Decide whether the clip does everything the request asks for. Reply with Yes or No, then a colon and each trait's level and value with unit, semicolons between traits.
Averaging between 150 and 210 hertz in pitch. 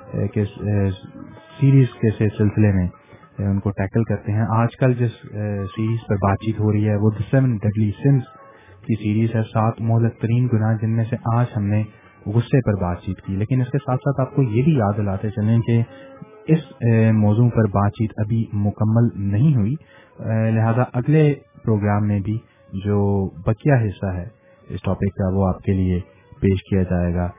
No: low, 110 Hz